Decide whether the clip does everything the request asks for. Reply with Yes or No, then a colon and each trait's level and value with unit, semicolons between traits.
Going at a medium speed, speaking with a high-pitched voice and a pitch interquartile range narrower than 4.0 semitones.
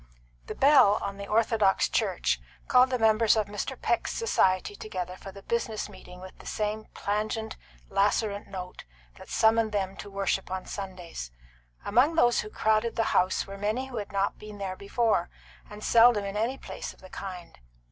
Yes: average, 180 wpm; high, 210 Hz; narrow, 2.5 semitones